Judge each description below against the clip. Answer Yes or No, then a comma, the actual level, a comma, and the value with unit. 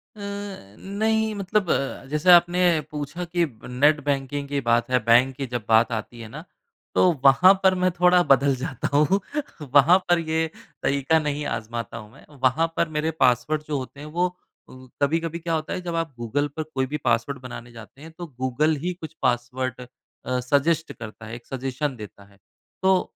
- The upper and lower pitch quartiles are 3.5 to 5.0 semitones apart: Yes, average, 4.6 semitones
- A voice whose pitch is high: No, medium, 145 Hz